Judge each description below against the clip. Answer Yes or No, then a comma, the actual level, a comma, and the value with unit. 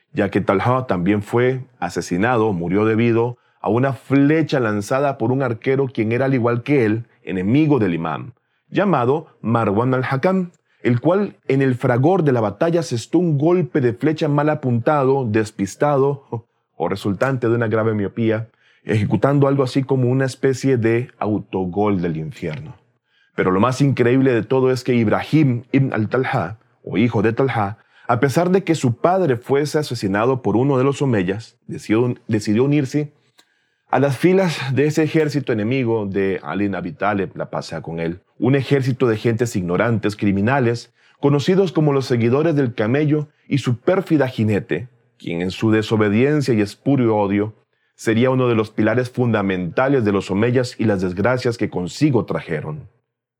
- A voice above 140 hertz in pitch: No, low, 120 Hz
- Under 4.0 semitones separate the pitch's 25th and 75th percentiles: No, average, 4.3 semitones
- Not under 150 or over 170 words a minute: Yes, average, 160 wpm